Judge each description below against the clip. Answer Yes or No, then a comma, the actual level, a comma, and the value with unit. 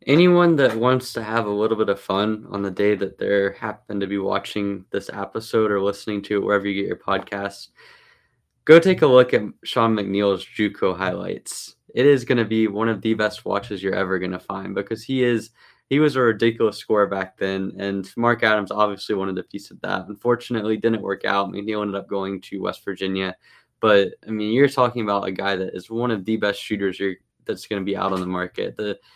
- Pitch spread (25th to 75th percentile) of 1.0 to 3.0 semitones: Yes, narrow, 2.5 semitones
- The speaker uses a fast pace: Yes, fast, 225 wpm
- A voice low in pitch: Yes, low, 105 Hz